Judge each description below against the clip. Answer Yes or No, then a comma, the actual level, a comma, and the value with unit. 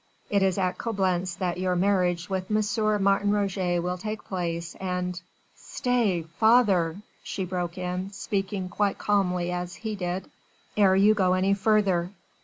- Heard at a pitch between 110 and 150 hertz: No, high, 190 Hz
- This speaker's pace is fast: No, average, 155 wpm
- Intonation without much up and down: Yes, narrow, 2.2 semitones